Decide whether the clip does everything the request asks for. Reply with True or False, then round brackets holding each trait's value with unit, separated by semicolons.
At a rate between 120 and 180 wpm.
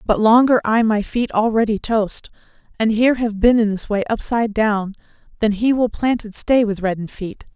False (190 wpm)